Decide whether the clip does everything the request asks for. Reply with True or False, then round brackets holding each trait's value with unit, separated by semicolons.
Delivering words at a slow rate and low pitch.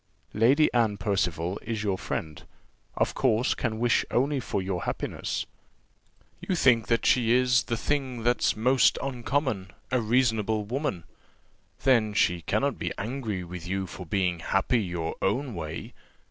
False (145 wpm; 110 Hz)